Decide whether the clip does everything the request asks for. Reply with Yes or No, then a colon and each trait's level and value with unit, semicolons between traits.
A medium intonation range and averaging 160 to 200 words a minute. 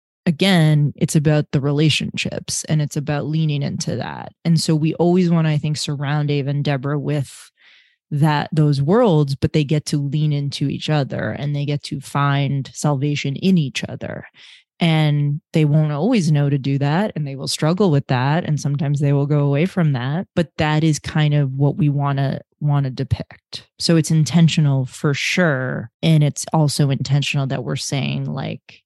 No: narrow, 1.9 semitones; average, 190 wpm